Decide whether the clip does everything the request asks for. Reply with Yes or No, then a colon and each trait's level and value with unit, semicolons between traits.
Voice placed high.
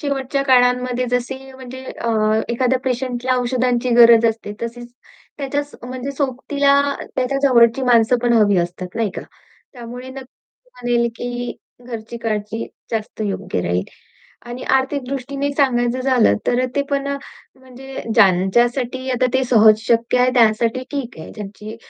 Yes: high, 245 Hz